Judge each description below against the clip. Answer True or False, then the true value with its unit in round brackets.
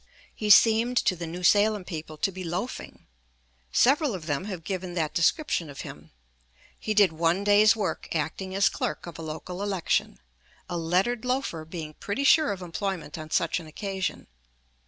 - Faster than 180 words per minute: False (175 wpm)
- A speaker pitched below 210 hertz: True (185 Hz)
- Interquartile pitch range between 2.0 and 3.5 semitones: False (4.2 semitones)